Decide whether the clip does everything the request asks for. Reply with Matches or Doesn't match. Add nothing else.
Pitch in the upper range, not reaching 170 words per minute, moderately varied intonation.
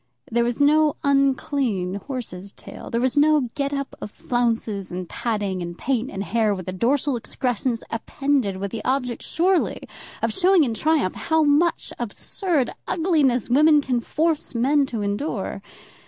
Matches